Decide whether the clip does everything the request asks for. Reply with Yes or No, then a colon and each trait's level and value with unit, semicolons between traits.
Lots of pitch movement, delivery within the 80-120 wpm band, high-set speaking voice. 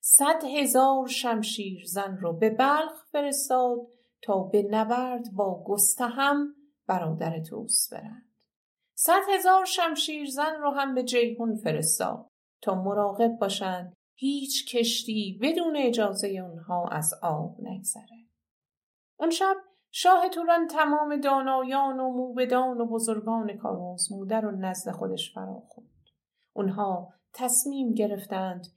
Yes: wide, 5.7 semitones; average, 115 wpm; high, 235 Hz